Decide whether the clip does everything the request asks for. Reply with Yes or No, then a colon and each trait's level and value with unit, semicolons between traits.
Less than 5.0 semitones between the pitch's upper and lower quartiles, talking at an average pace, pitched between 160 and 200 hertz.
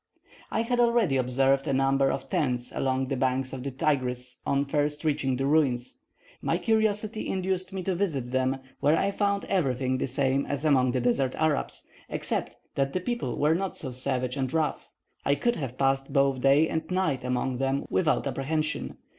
No: average, 3.6 semitones; average, 185 wpm; medium, 140 Hz